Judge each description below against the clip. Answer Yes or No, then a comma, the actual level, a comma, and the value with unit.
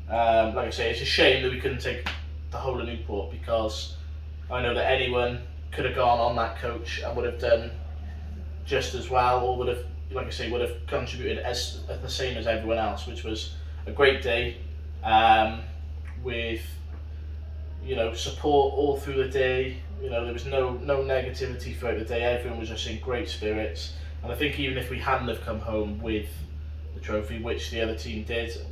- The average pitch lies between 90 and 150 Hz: No, very low, 80 Hz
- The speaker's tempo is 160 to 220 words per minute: Yes, fast, 205 wpm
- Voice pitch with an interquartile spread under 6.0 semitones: No, wide, 6.8 semitones